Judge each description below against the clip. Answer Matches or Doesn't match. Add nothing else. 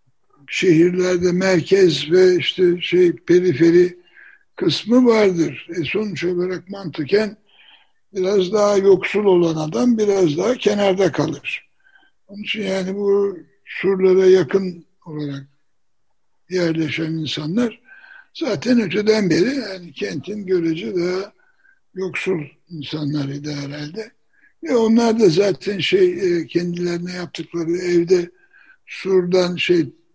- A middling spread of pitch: Matches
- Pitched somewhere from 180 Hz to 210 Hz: Matches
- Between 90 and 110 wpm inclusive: Matches